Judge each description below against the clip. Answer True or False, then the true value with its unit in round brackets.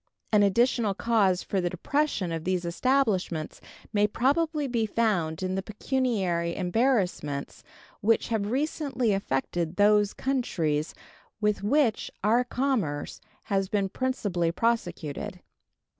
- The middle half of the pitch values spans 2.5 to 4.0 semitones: False (5.6 semitones)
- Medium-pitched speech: False (205 Hz)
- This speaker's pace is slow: True (115 wpm)